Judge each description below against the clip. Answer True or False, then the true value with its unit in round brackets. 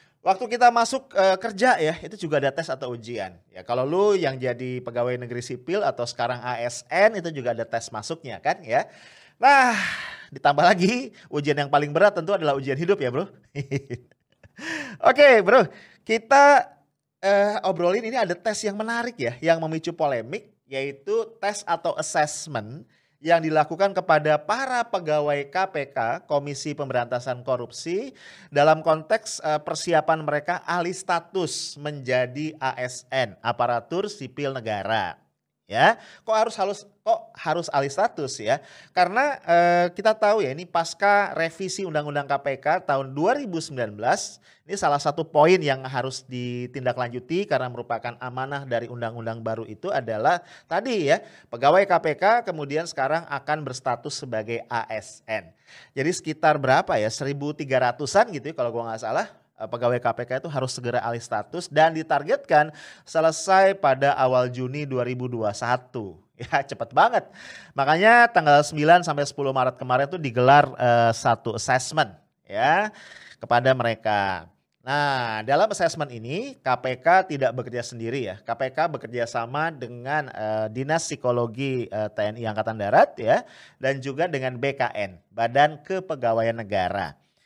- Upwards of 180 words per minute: False (135 wpm)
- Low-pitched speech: False (145 Hz)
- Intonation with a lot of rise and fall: True (5.7 semitones)